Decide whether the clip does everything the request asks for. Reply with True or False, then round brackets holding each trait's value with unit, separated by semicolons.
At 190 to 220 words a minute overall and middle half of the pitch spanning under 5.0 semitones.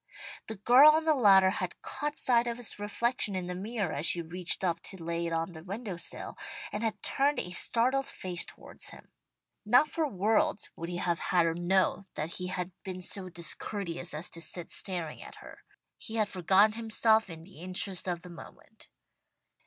True (195 wpm; 4.2 semitones)